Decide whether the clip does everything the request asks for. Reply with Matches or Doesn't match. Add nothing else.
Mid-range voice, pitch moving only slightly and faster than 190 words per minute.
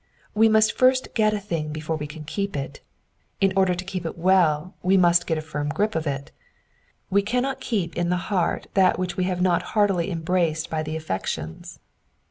Doesn't match